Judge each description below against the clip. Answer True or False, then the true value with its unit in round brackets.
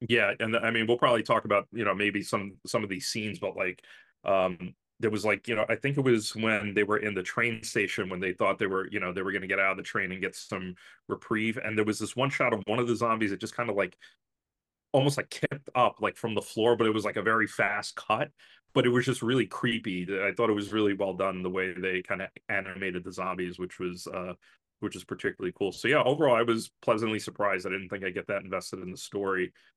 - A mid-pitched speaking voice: False (105 Hz)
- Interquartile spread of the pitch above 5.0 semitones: False (3.0 semitones)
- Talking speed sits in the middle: False (270 wpm)